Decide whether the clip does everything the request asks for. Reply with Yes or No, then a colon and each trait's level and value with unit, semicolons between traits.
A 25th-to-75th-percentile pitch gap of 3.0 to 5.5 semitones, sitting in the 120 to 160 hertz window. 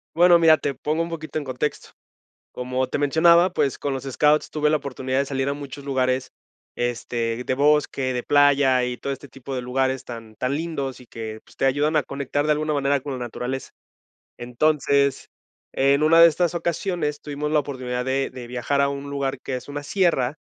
No: narrow, 2.6 semitones; medium, 140 Hz